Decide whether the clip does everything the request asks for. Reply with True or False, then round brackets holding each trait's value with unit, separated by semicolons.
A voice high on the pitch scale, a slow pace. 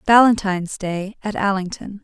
True (200 Hz; 120 wpm)